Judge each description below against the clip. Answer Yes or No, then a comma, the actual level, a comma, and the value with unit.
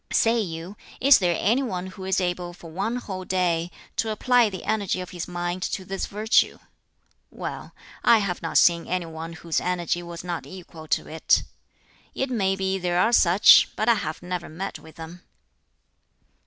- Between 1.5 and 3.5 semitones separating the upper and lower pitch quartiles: Yes, narrow, 2.6 semitones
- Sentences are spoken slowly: No, average, 180 wpm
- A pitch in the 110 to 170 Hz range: No, medium, 180 Hz